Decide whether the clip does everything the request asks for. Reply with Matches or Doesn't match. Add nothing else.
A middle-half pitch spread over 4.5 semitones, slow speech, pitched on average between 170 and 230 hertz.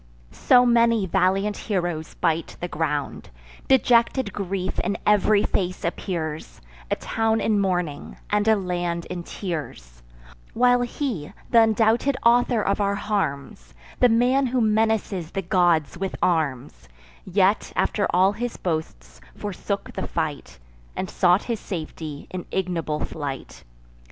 Matches